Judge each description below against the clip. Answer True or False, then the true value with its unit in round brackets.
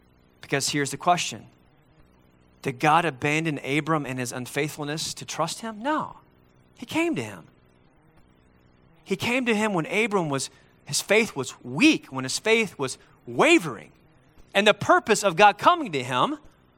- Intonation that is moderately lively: False (8.6 semitones)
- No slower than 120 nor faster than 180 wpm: True (155 wpm)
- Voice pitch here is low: False (155 Hz)